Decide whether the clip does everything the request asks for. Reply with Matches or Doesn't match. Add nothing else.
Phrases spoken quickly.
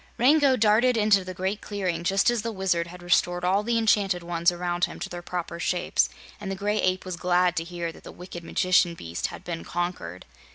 Matches